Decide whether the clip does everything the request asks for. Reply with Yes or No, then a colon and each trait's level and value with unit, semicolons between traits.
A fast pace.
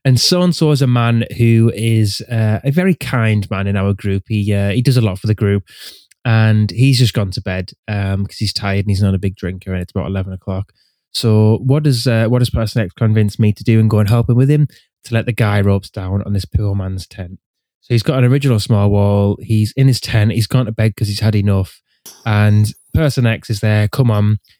Yes: fast, 250 wpm